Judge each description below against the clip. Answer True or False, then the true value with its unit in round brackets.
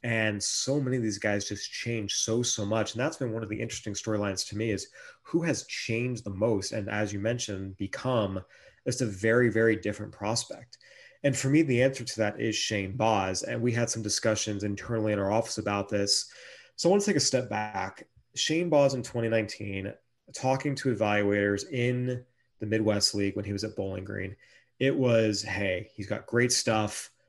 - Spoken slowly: False (200 wpm)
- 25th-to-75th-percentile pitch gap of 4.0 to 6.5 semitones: False (3.2 semitones)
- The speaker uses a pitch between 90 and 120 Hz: True (110 Hz)